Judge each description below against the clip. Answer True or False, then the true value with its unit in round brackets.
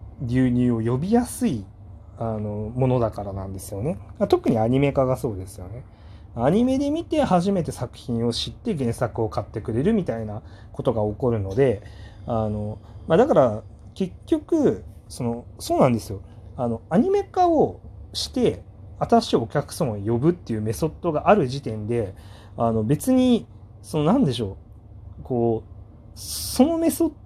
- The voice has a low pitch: True (115 Hz)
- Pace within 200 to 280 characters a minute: False (305 characters per minute)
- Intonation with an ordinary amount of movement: False (6.3 semitones)